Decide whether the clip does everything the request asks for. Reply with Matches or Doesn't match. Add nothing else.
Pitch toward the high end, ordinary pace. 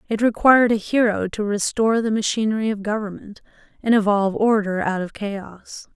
Matches